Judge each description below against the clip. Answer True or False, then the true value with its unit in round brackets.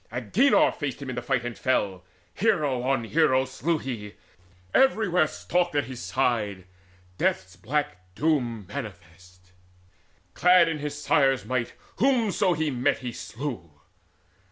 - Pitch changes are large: True (5.9 semitones)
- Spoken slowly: True (130 wpm)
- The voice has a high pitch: False (130 Hz)